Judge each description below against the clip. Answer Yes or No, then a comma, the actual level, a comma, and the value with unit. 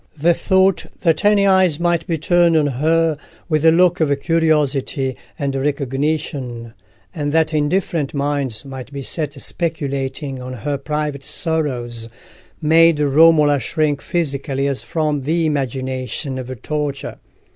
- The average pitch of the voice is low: No, medium, 150 Hz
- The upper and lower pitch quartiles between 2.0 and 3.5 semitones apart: Yes, average, 3.0 semitones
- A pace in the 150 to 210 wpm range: No, slow, 135 wpm